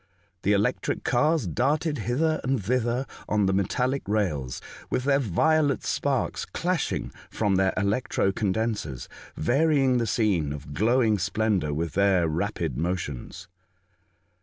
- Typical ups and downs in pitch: No, wide, 5.9 semitones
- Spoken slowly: Yes, slow, 125 wpm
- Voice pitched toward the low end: Yes, low, 110 Hz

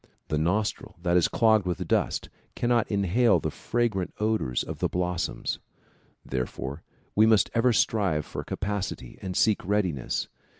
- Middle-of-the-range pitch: No, low, 100 Hz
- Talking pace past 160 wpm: No, average, 140 wpm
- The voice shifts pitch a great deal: No, average, 4.0 semitones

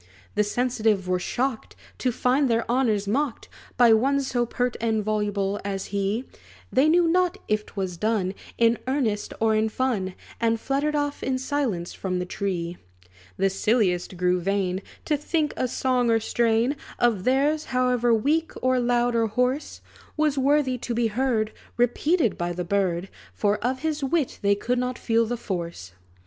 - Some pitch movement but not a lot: Yes, average, 4.5 semitones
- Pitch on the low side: No, high, 235 Hz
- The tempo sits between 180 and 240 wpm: No, average, 170 wpm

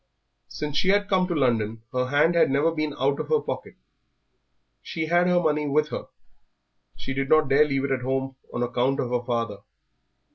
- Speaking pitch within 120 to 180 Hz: Yes, medium, 140 Hz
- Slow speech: No, average, 195 wpm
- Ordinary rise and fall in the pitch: Yes, average, 3.7 semitones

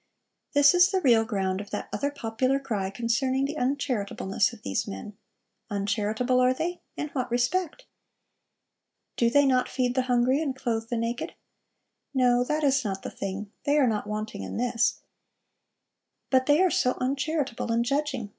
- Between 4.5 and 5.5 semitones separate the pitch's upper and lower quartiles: No, average, 4.0 semitones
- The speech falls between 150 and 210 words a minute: Yes, average, 165 wpm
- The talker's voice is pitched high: Yes, very high, 250 Hz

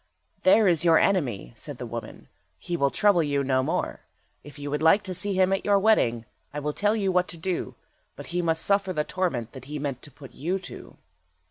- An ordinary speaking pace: No, fast, 225 wpm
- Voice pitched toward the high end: No, medium, 165 Hz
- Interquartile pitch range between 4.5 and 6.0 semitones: Yes, average, 5.1 semitones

